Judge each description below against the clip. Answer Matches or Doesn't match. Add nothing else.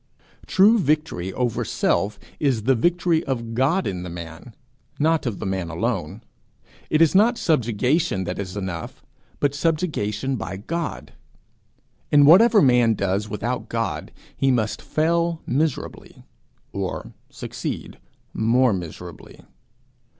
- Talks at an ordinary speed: Doesn't match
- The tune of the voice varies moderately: Doesn't match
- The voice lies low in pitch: Matches